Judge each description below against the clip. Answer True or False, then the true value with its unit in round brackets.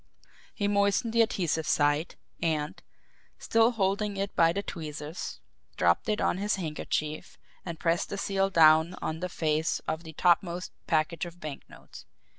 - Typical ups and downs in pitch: True (4.0 semitones)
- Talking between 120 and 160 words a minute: True (150 wpm)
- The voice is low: False (170 Hz)